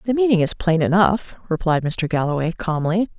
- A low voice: No, medium, 180 Hz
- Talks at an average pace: Yes, average, 170 wpm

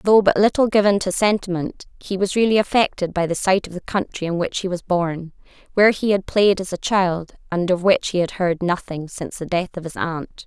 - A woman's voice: Yes, female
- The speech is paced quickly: Yes, fast, 230 wpm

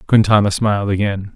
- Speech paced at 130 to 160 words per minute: Yes, slow, 135 wpm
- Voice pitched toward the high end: No, low, 105 Hz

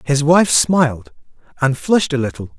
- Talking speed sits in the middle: Yes, average, 165 wpm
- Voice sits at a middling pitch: Yes, medium, 145 Hz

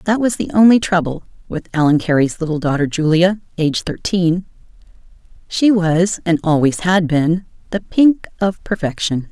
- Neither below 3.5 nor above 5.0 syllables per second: Yes, 4.9 syllables/s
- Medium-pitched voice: Yes, medium, 175 Hz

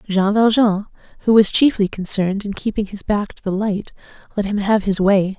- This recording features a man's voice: No, female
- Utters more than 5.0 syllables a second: Yes, 5.2 syllables/s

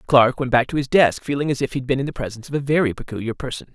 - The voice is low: Yes, low, 130 Hz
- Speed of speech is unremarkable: No, fast, 320 wpm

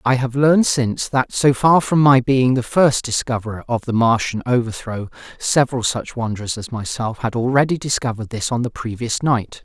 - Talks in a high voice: No, low, 125 Hz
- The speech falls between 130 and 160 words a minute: No, average, 185 wpm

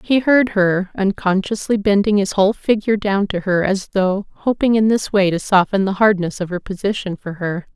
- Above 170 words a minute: Yes, average, 200 wpm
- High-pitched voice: Yes, high, 200 Hz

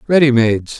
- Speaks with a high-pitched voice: No, low, 130 Hz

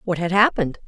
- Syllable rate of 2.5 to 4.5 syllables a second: No, 7.0 syllables/s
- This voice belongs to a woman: Yes, female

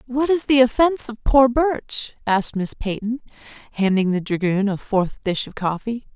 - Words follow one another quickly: No, average, 175 wpm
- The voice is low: No, high, 230 Hz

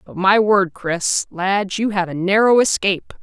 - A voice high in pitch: Yes, high, 195 Hz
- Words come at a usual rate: Yes, average, 185 wpm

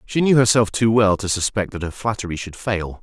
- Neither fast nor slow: No, fast, 240 wpm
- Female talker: No, male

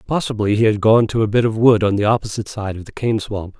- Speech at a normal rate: No, fast, 285 wpm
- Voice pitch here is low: Yes, low, 105 Hz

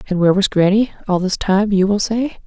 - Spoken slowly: No, fast, 245 wpm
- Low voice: No, high, 200 Hz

